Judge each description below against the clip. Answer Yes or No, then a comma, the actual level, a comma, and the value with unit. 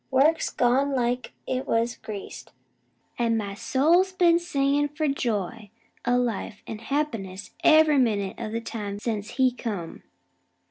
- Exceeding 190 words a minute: No, average, 140 wpm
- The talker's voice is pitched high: Yes, high, 245 Hz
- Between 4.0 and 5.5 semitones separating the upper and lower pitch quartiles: Yes, average, 4.7 semitones